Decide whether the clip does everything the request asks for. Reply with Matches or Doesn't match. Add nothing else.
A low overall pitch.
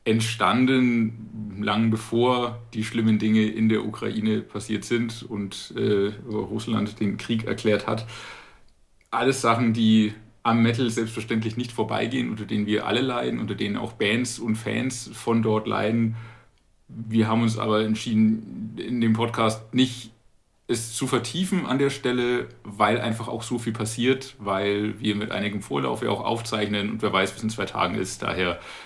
Matches